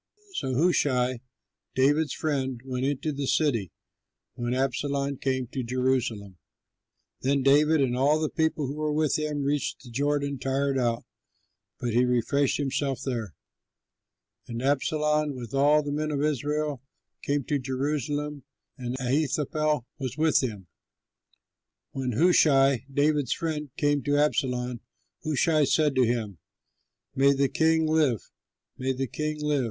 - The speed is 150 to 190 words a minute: No, slow, 135 wpm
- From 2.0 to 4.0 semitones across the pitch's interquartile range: Yes, average, 2.7 semitones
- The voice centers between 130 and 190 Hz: Yes, medium, 140 Hz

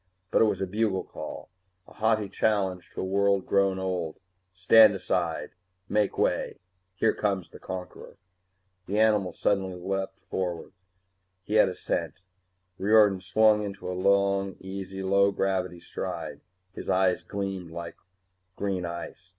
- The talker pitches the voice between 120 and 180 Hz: No, very low, 95 Hz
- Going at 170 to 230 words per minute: No, average, 140 wpm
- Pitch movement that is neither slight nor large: No, narrow, 1.6 semitones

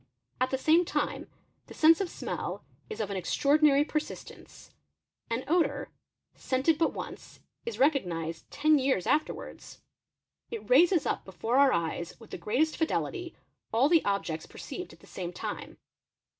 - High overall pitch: Yes, very high, 275 Hz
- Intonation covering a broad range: Yes, wide, 7.7 semitones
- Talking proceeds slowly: No, average, 155 wpm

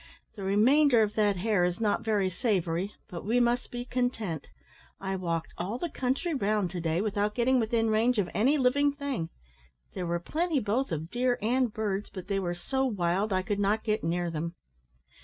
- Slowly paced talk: No, average, 195 wpm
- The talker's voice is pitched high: Yes, high, 210 Hz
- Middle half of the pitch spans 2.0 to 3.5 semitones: No, average, 5.1 semitones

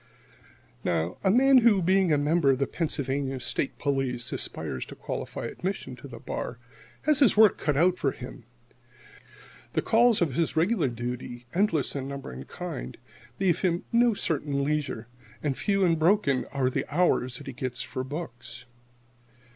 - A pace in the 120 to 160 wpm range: No, average, 170 wpm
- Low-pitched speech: No, medium, 145 Hz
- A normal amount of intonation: No, wide, 6.4 semitones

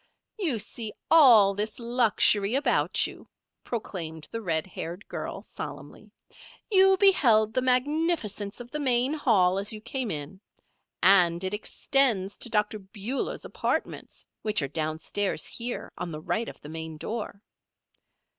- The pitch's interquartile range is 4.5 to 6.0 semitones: Yes, average, 4.9 semitones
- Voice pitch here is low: No, high, 215 Hz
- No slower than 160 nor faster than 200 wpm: No, average, 140 wpm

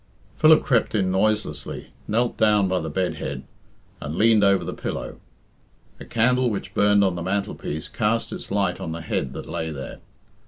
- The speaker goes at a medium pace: Yes, average, 180 wpm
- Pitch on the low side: Yes, low, 100 Hz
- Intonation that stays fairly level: No, average, 4.0 semitones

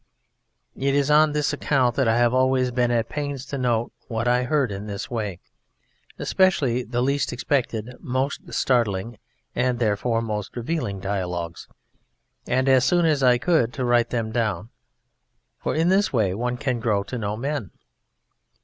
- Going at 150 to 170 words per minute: Yes, average, 165 wpm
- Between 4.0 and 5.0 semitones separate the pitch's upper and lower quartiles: No, average, 3.4 semitones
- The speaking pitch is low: Yes, low, 125 Hz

